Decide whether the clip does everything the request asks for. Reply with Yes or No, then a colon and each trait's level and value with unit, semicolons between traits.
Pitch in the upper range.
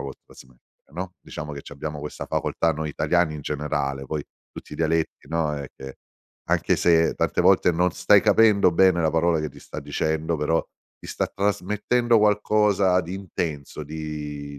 No: very low, 80 Hz